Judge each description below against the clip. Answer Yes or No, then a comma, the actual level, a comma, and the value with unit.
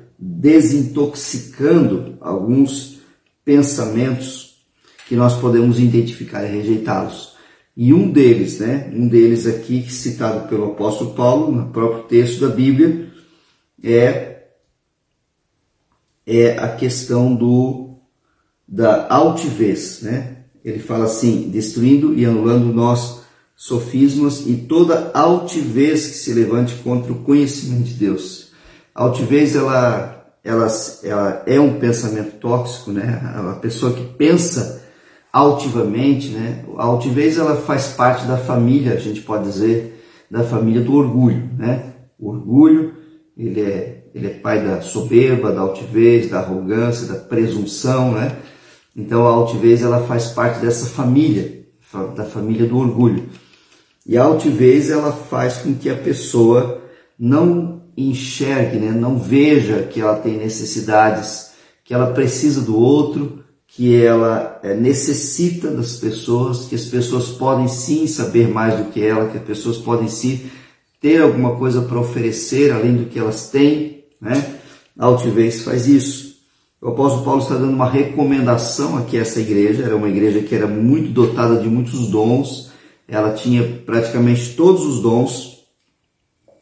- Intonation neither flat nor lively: Yes, average, 3.2 semitones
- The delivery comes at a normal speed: Yes, average, 135 wpm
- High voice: No, low, 120 Hz